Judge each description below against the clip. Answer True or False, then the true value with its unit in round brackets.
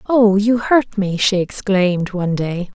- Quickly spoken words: False (150 wpm)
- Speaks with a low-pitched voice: False (200 Hz)